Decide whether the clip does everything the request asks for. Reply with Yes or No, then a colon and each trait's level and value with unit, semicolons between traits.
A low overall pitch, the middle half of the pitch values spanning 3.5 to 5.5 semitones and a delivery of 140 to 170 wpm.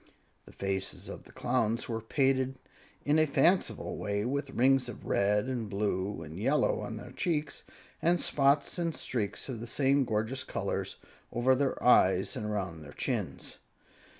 Yes: low, 120 Hz; average, 4.9 semitones; average, 160 wpm